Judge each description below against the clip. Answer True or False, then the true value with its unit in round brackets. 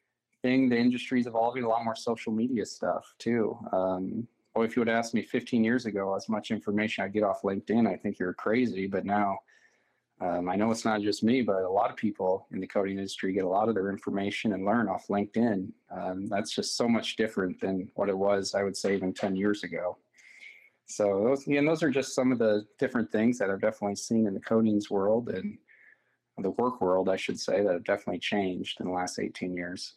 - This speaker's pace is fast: True (225 wpm)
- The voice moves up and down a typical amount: True (3.0 semitones)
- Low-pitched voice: True (105 Hz)